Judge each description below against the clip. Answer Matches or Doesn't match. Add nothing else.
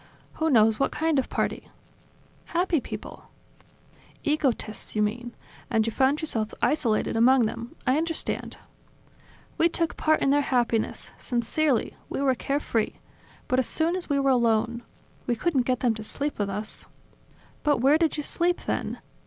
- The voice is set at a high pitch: Matches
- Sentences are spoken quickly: Doesn't match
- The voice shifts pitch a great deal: Doesn't match